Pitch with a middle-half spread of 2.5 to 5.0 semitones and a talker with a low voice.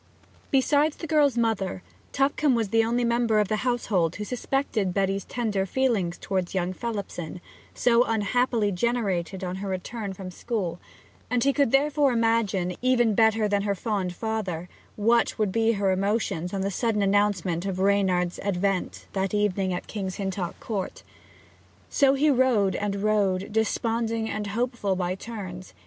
No: average, 3.6 semitones; high, 210 Hz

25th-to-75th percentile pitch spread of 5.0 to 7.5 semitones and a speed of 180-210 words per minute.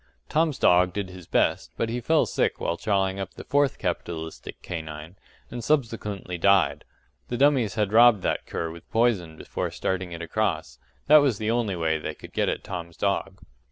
Yes: wide, 5.5 semitones; average, 185 wpm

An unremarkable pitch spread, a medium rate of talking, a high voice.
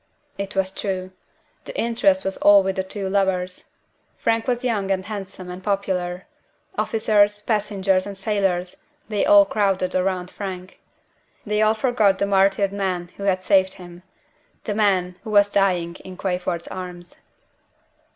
No: narrow, 1.9 semitones; average, 150 wpm; high, 195 Hz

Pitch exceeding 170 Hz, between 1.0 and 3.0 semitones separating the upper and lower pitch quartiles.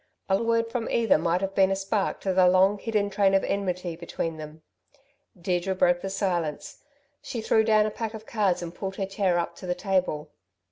Yes: high, 190 Hz; average, 2.7 semitones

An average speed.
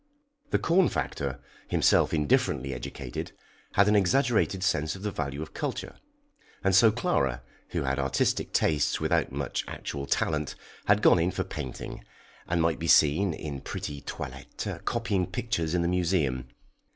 Yes: average, 150 wpm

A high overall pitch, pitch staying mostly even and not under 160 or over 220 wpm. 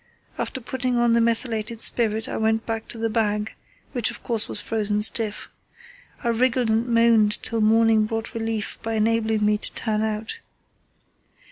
Yes: high, 225 Hz; narrow, 1.2 semitones; average, 165 wpm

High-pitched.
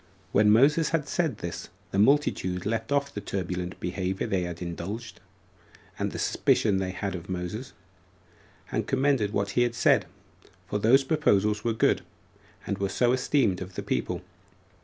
No: low, 105 Hz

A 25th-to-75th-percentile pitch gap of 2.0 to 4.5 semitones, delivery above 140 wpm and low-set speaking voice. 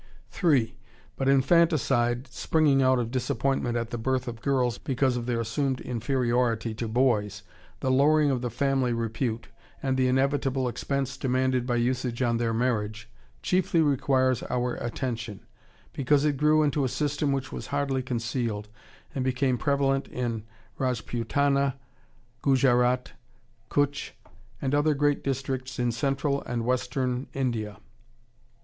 No: narrow, 2.5 semitones; slow, 135 wpm; low, 130 Hz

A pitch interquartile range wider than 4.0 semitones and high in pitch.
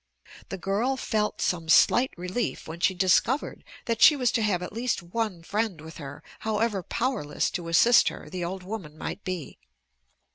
Yes: average, 4.9 semitones; high, 195 Hz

